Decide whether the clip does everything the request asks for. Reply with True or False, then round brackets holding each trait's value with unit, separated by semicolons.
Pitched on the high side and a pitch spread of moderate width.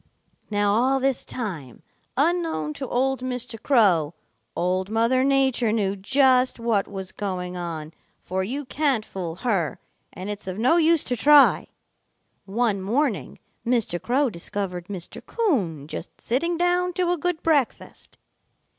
False (230 Hz; 6.2 semitones)